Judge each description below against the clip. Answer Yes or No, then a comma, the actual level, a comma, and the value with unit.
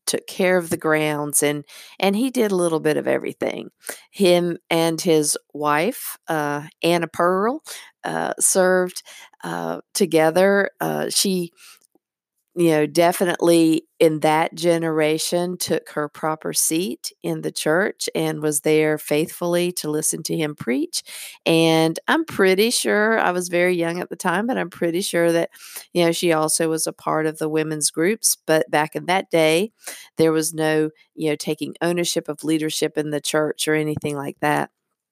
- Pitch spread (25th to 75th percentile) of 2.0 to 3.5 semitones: Yes, average, 2.7 semitones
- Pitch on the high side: No, medium, 165 Hz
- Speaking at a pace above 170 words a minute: No, average, 165 wpm